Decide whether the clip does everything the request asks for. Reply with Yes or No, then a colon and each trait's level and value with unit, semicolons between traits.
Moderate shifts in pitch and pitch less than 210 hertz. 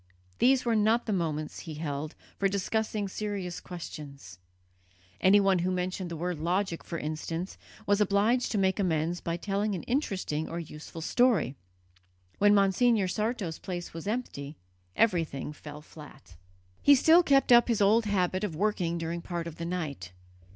Yes: average, 4.4 semitones; medium, 185 Hz